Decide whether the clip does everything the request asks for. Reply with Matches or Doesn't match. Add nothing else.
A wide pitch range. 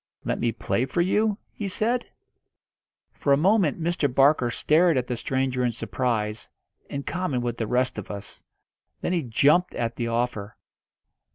Matches